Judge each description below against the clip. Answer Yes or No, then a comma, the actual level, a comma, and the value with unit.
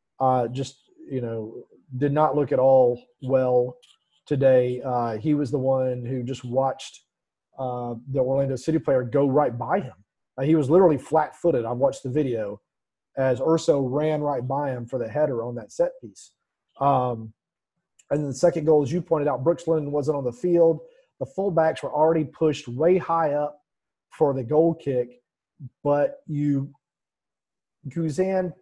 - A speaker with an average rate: Yes, average, 170 wpm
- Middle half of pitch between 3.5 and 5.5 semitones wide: Yes, average, 3.9 semitones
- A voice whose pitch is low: No, medium, 145 Hz